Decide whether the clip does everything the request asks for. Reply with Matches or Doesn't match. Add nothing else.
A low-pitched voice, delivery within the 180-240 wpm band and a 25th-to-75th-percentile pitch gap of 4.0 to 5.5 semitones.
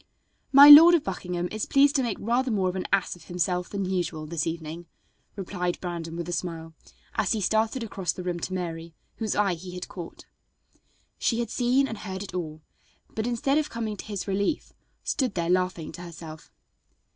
Doesn't match